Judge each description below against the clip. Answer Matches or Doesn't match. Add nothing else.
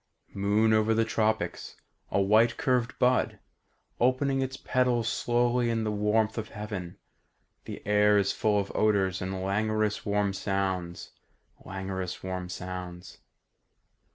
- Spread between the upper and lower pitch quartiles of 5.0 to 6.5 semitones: Doesn't match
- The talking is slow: Matches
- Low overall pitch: Matches